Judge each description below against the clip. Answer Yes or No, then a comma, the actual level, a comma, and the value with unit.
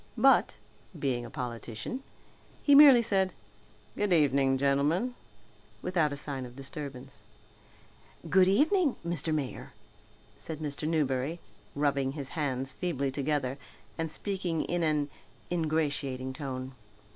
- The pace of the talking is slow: Yes, slow, 115 wpm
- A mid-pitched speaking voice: Yes, medium, 145 Hz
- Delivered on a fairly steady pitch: No, average, 4.4 semitones